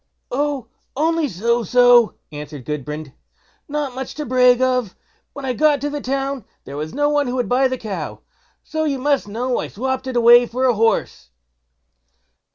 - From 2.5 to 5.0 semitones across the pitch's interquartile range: Yes, average, 3.3 semitones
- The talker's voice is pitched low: No, very high, 255 Hz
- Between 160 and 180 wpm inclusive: Yes, average, 175 wpm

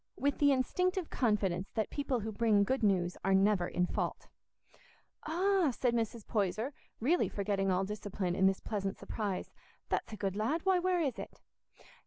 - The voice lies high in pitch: Yes, high, 215 Hz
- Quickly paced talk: No, average, 170 wpm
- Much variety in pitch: Yes, wide, 6.3 semitones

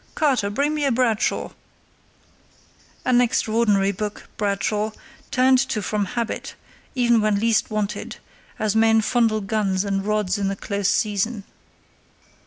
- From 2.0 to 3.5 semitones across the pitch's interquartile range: Yes, average, 2.8 semitones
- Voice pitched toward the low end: No, high, 215 Hz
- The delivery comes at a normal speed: No, slow, 125 wpm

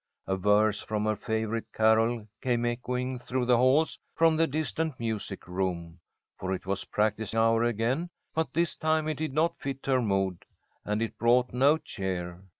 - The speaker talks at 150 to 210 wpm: Yes, average, 170 wpm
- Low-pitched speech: Yes, low, 115 Hz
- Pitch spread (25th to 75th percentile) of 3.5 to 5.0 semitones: Yes, average, 4.3 semitones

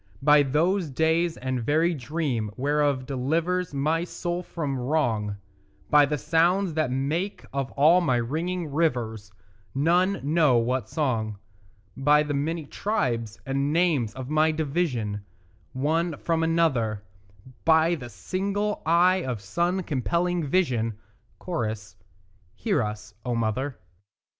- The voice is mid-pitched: Yes, medium, 150 Hz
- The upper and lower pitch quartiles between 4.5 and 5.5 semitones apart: Yes, average, 5.1 semitones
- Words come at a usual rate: No, slow, 125 wpm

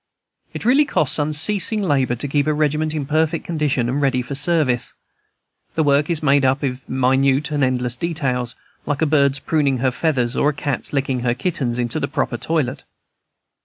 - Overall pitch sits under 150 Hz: Yes, medium, 140 Hz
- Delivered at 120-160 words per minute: No, average, 185 wpm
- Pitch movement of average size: Yes, average, 3.1 semitones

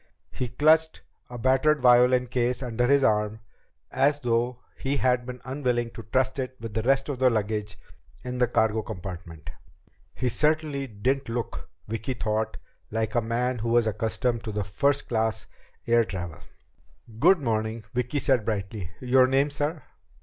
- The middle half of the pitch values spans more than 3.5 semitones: No, average, 3.1 semitones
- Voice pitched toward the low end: Yes, low, 120 Hz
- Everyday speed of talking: Yes, average, 155 wpm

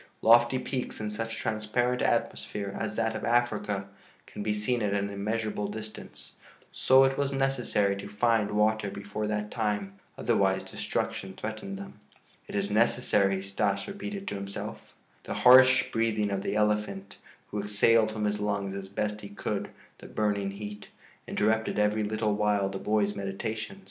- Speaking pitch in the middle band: No, low, 105 Hz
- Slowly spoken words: No, average, 160 wpm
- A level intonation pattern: Yes, narrow, 2.0 semitones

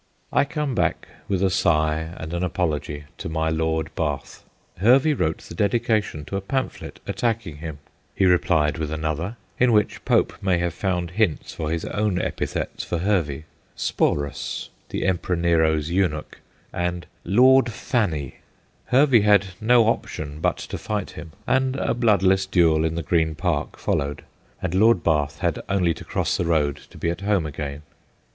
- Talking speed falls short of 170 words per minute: No, average, 175 wpm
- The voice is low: Yes, very low, 85 Hz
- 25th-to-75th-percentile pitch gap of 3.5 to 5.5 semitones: Yes, average, 4.7 semitones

